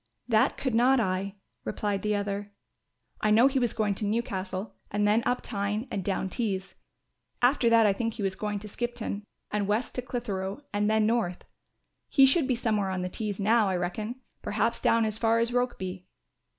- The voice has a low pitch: No, high, 210 Hz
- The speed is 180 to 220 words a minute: Yes, average, 190 wpm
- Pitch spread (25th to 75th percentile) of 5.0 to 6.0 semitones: No, average, 2.9 semitones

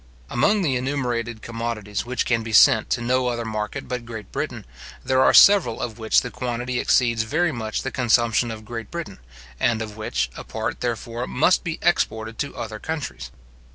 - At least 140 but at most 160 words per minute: No, average, 185 wpm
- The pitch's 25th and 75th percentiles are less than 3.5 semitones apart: Yes, narrow, 2.4 semitones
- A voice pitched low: Yes, low, 120 Hz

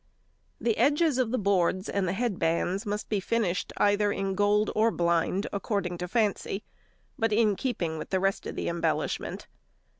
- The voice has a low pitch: No, high, 200 Hz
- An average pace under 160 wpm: No, average, 175 wpm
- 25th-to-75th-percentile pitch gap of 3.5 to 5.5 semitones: No, average, 3.0 semitones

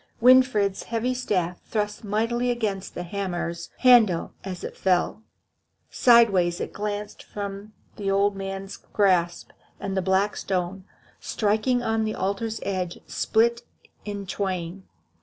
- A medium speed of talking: No, slow, 125 wpm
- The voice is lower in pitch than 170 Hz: No, high, 200 Hz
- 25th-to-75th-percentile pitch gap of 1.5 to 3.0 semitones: Yes, average, 2.7 semitones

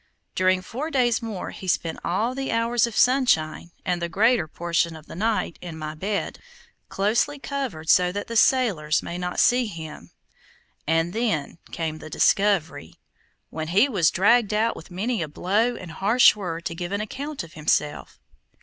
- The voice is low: No, high, 190 Hz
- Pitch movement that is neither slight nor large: No, wide, 5.9 semitones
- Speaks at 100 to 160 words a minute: No, average, 175 wpm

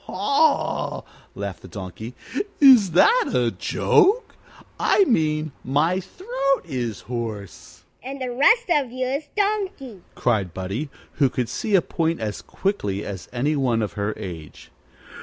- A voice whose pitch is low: No, medium, 155 Hz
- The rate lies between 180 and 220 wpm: No, average, 145 wpm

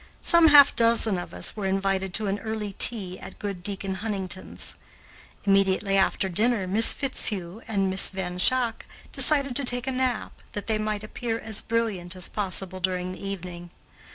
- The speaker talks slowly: No, average, 170 wpm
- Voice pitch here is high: Yes, high, 200 Hz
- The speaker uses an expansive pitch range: No, average, 3.3 semitones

